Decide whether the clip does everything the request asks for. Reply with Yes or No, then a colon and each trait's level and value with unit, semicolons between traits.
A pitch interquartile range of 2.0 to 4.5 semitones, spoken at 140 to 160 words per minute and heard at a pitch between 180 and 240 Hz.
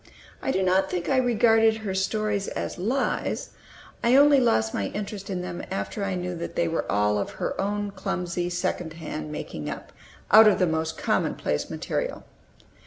No: average, 4.0 semitones; average, 175 wpm; high, 190 Hz